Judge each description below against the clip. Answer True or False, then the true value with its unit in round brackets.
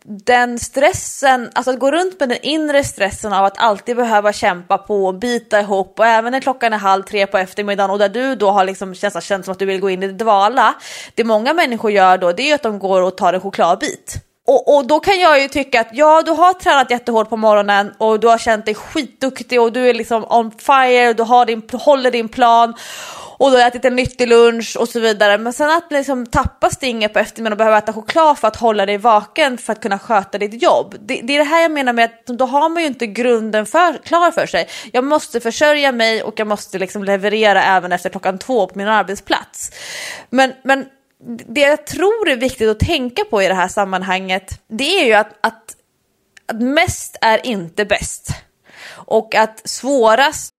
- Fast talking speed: True (220 wpm)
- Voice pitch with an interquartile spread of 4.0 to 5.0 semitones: True (4.4 semitones)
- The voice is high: True (230 Hz)